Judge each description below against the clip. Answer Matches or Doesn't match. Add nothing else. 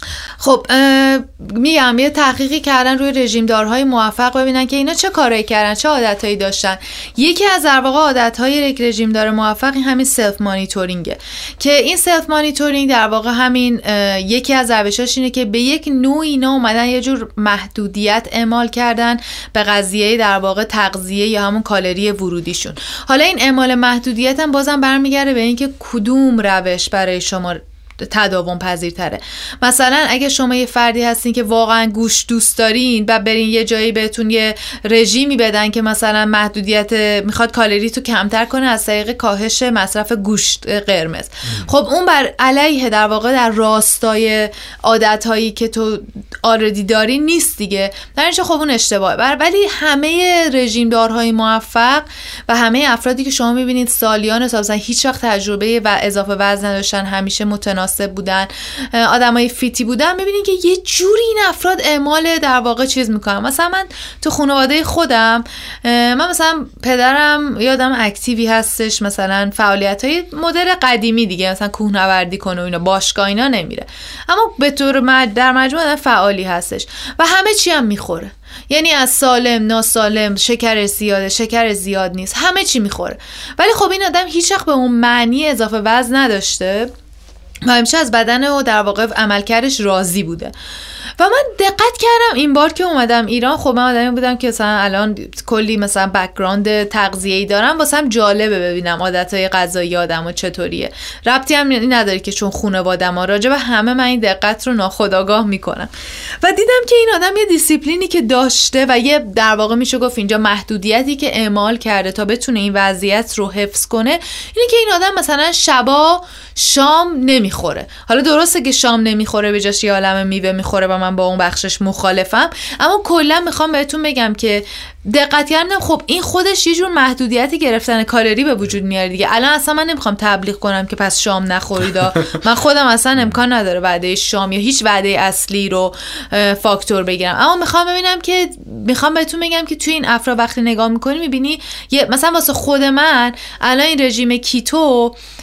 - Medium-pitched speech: Doesn't match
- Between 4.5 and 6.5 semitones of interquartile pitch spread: Matches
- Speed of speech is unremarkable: Doesn't match